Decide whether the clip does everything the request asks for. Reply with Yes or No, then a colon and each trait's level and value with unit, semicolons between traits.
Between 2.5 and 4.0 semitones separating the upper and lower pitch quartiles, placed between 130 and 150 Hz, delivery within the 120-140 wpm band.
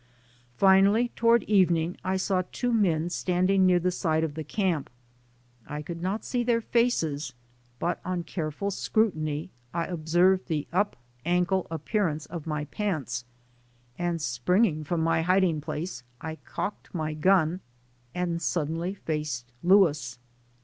No: average, 3.5 semitones; medium, 175 Hz; slow, 135 wpm